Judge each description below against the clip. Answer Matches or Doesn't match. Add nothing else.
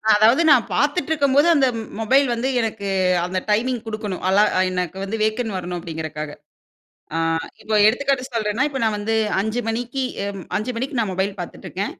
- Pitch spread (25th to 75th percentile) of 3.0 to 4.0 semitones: Doesn't match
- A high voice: Matches